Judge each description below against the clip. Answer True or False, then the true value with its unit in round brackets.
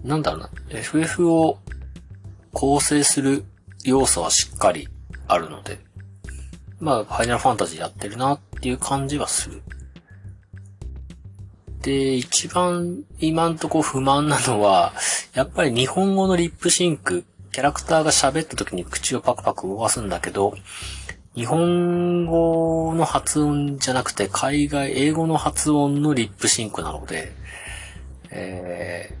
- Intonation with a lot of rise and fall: True (7.9 semitones)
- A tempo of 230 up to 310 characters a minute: True (270 characters per minute)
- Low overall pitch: True (130 Hz)